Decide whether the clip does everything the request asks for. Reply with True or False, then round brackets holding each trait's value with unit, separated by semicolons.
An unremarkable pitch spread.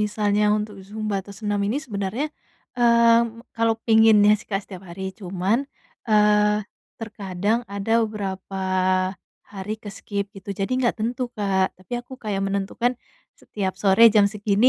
False (2.2 semitones)